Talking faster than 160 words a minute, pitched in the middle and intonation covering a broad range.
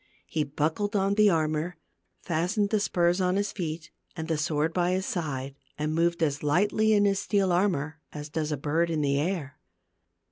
No: average, 185 wpm; medium, 165 Hz; average, 4.0 semitones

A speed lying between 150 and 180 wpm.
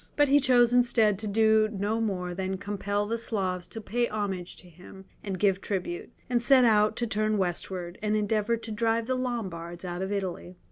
No: average, 195 wpm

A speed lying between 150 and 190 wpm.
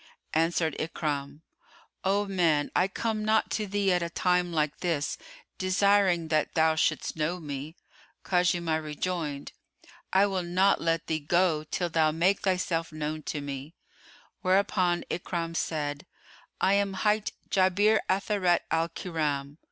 No: slow, 135 wpm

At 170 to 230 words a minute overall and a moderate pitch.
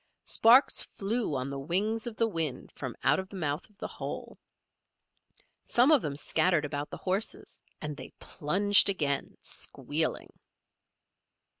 No: average, 145 wpm; medium, 180 Hz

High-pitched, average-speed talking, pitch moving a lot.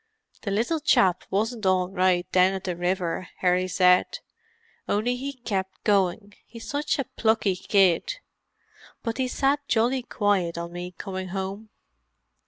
No: high, 195 Hz; average, 145 wpm; average, 4.0 semitones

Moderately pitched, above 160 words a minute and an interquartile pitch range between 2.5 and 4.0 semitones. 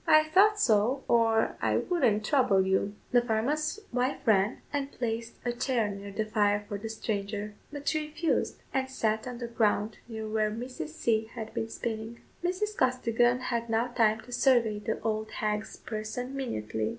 No: high, 230 Hz; average, 175 wpm; average, 3.1 semitones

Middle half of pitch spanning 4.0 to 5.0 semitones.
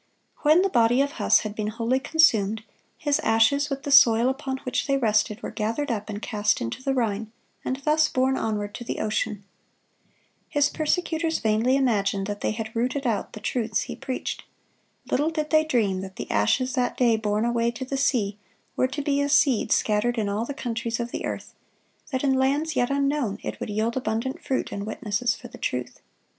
Yes: average, 4.3 semitones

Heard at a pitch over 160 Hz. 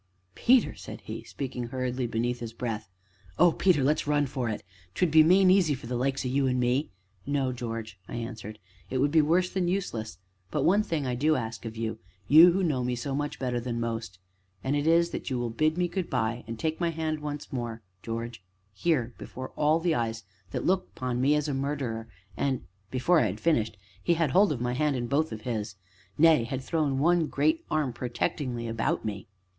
No: low, 130 Hz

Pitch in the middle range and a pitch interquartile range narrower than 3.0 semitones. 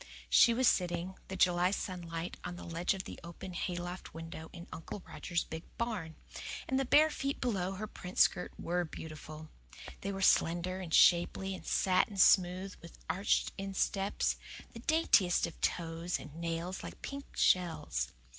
Yes: medium, 180 Hz; narrow, 2.4 semitones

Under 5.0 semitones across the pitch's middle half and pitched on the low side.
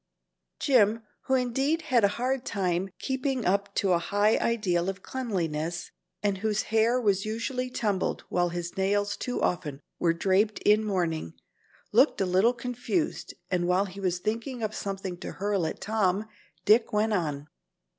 No: average, 4.2 semitones; high, 205 Hz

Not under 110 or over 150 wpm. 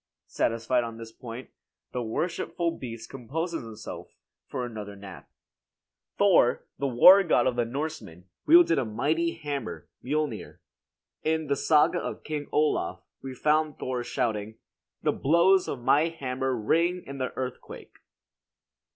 Yes: slow, 135 wpm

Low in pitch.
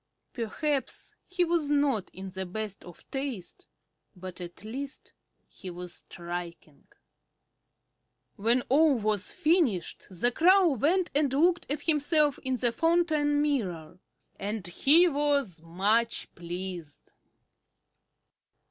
No: high, 245 Hz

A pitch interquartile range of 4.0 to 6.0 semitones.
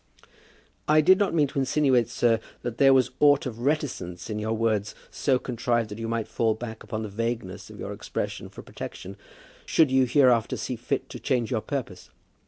No: average, 3.5 semitones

